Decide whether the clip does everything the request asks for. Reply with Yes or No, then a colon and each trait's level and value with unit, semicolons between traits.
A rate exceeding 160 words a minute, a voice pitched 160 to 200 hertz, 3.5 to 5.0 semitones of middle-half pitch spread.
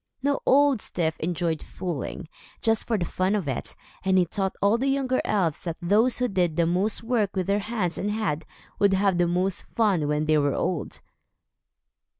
Yes: average, 190 wpm; high, 190 Hz; average, 4.2 semitones